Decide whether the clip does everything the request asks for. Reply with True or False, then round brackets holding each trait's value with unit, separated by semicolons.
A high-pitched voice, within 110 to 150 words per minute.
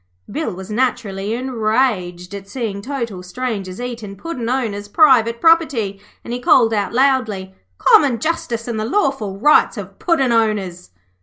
True (230 Hz; 145 wpm)